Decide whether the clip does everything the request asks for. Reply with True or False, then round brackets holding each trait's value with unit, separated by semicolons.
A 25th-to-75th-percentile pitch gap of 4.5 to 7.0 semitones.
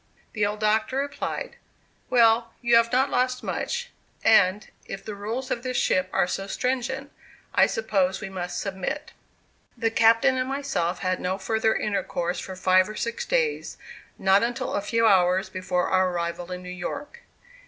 True (5.5 semitones)